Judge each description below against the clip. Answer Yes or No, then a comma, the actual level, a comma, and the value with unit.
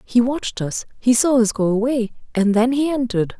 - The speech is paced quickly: Yes, fast, 210 wpm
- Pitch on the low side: No, high, 235 Hz